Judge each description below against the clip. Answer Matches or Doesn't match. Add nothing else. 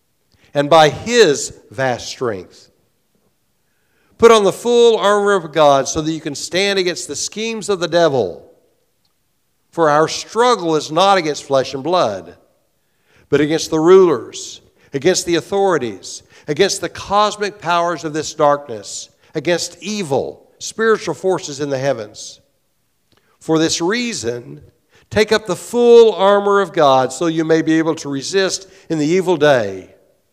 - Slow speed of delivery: Doesn't match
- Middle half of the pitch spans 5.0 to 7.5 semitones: Matches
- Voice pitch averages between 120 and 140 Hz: Doesn't match